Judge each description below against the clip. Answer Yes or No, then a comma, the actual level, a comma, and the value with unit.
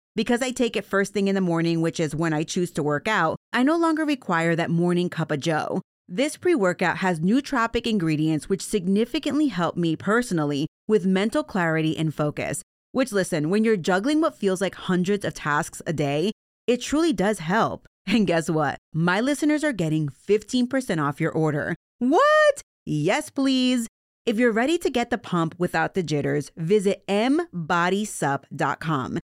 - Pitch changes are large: Yes, wide, 6.7 semitones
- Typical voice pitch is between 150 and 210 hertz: Yes, high, 190 Hz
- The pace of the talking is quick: No, average, 170 wpm